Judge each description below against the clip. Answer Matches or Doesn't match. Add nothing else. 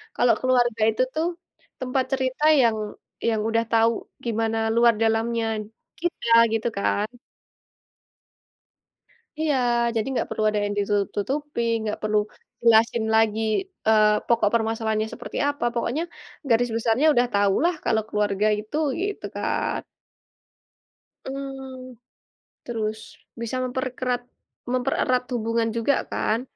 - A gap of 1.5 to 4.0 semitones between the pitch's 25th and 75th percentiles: Matches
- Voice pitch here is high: Matches